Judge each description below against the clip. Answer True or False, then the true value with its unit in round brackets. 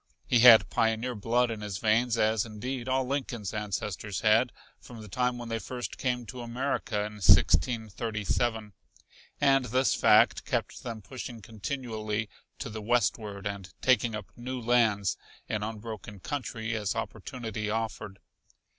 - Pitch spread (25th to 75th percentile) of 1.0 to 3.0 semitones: True (2.6 semitones)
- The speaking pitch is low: True (115 Hz)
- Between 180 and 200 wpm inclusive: False (145 wpm)